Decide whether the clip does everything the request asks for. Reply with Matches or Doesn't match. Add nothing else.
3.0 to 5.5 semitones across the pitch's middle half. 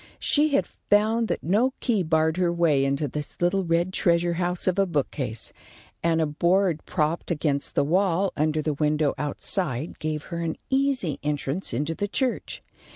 Matches